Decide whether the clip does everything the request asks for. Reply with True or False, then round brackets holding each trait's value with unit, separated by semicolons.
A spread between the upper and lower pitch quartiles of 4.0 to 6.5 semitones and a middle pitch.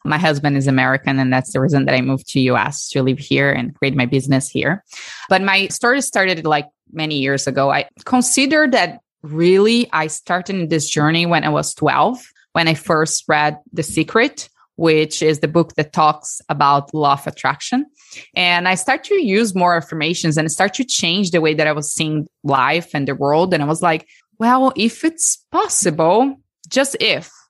True (5.0 semitones; 160 Hz)